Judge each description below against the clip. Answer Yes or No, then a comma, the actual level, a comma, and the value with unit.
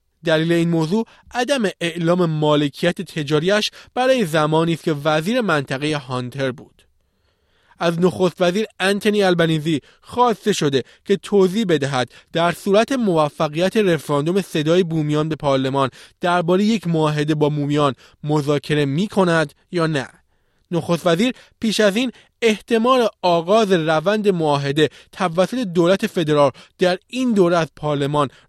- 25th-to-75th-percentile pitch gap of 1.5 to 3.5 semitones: No, average, 4.7 semitones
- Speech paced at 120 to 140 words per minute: Yes, average, 125 wpm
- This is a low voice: No, medium, 170 Hz